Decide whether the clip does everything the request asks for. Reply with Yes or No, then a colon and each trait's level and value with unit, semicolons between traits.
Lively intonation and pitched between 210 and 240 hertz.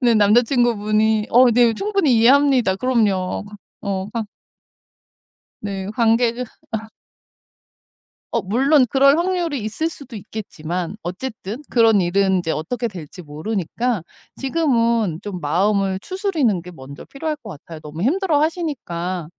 Yes: wide, 5.8 semitones; high, 225 Hz